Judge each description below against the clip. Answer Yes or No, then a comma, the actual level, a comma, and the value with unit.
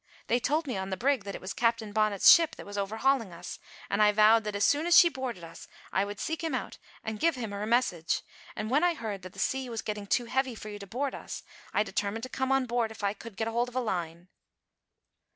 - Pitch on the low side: No, high, 220 Hz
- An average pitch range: Yes, average, 4.2 semitones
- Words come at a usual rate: No, fast, 260 wpm